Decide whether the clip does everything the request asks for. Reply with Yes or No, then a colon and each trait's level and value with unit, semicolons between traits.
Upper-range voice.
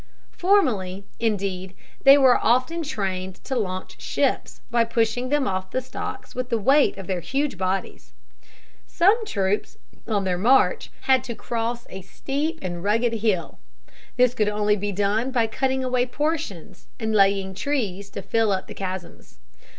Yes: high, 220 Hz